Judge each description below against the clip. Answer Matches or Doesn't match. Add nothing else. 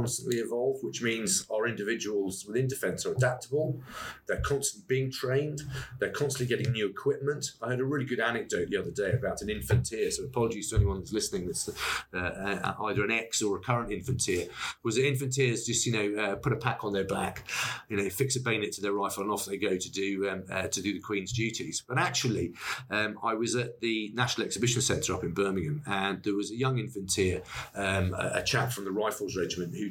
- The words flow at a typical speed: Doesn't match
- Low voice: Matches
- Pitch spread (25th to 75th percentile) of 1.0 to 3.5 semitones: Doesn't match